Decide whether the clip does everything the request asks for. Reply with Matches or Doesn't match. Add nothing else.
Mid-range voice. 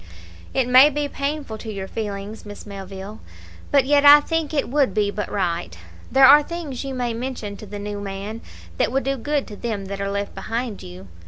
Doesn't match